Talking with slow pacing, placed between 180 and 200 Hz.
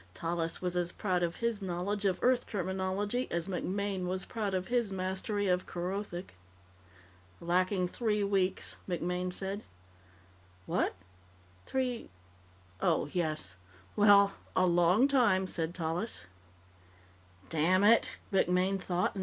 Yes: slow, 105 wpm; medium, 185 Hz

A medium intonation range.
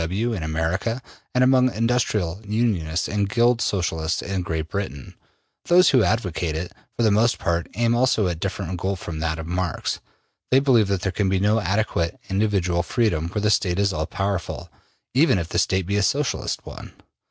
Yes: average, 4.7 semitones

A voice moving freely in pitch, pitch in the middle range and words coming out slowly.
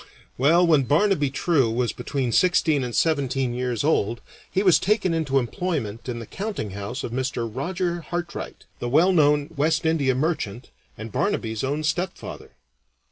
No: wide, 5.8 semitones; medium, 145 Hz; average, 150 wpm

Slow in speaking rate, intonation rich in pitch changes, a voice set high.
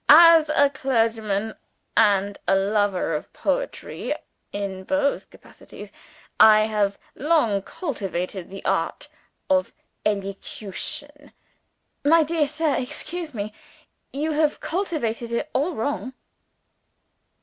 Yes: slow, 105 wpm; wide, 6.8 semitones; high, 245 Hz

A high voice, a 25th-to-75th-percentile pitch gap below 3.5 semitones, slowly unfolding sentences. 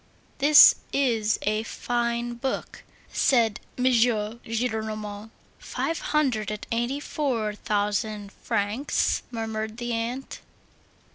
Yes: high, 230 Hz; narrow, 2.5 semitones; slow, 95 wpm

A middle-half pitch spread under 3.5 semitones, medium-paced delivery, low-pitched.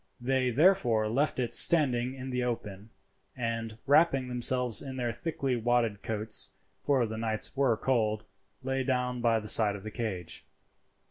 Yes: average, 3.0 semitones; average, 155 wpm; low, 120 Hz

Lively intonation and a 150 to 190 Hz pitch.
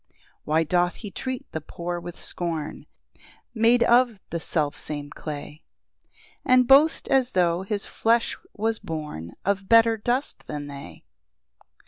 Yes: wide, 6.8 semitones; medium, 185 Hz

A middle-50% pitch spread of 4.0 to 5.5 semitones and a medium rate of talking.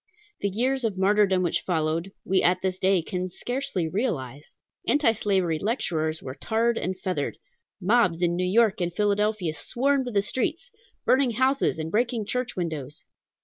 Yes: average, 5.2 semitones; average, 155 wpm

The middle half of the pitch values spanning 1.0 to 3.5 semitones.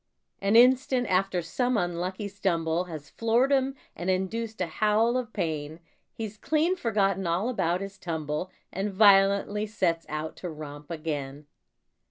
No: average, 4.8 semitones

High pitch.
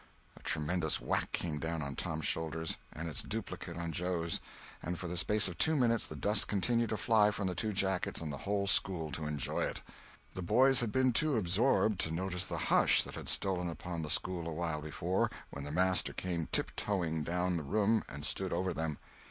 No: very low, 90 Hz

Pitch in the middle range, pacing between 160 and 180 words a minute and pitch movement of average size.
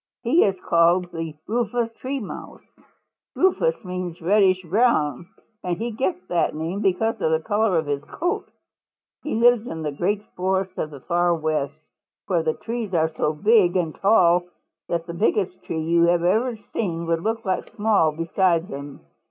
Yes: medium, 180 Hz; average, 170 wpm; average, 4.5 semitones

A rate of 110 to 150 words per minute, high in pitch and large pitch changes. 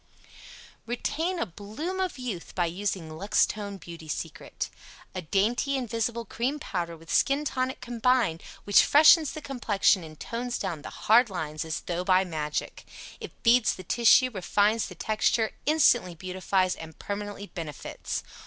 Yes: average, 145 wpm; high, 205 Hz; wide, 5.7 semitones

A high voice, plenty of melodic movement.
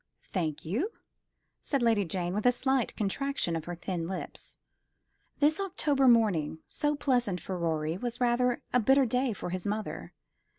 Yes: high, 225 Hz; wide, 6.8 semitones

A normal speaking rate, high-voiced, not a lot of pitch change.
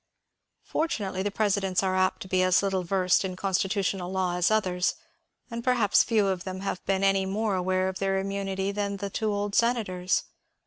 Yes: average, 185 wpm; high, 195 Hz; narrow, 1.5 semitones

